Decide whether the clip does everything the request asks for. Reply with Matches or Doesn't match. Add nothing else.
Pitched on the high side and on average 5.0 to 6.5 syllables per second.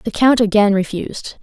Matches